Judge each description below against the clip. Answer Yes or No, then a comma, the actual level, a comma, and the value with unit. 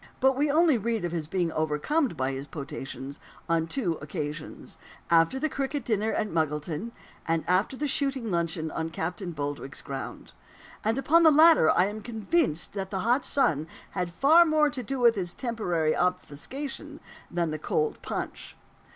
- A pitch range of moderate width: No, wide, 9.0 semitones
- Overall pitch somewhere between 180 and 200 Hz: Yes, high, 190 Hz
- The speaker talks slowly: No, average, 170 wpm